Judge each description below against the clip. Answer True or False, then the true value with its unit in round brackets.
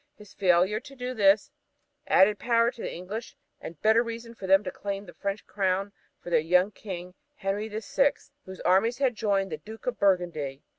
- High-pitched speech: True (200 Hz)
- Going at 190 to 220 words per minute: True (200 wpm)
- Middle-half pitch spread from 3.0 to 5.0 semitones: True (3.4 semitones)